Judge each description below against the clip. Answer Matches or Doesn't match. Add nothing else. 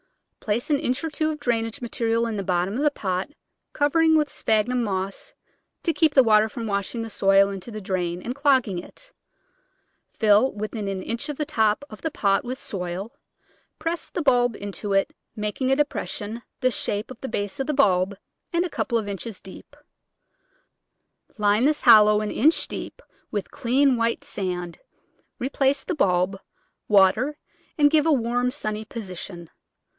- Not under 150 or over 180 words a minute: Matches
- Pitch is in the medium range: Doesn't match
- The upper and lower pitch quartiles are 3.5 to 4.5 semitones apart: Doesn't match